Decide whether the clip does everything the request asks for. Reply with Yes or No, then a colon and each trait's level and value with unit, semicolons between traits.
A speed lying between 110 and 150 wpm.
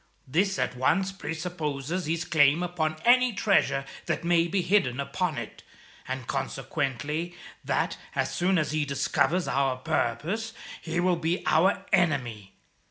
Yes: average, 140 wpm